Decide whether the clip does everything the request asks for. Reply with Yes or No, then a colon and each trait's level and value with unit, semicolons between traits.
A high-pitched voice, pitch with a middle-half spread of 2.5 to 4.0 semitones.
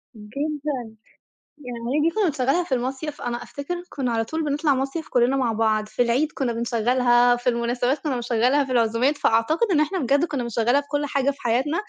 Yes: very high, 260 Hz; average, 3.5 semitones